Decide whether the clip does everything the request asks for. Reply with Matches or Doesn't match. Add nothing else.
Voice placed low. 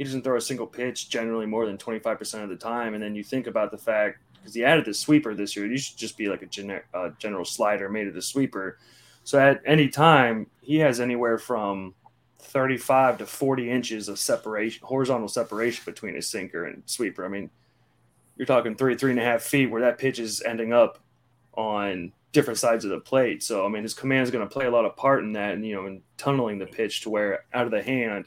Matches